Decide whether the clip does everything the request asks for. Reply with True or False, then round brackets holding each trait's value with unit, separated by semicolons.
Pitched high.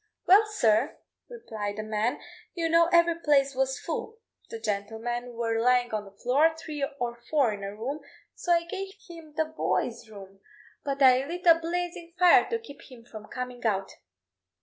True (265 Hz)